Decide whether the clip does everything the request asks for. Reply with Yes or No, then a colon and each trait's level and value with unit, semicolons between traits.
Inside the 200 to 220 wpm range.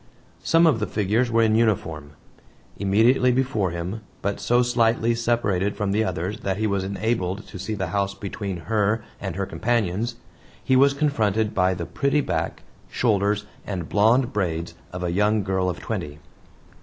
No: average, 170 wpm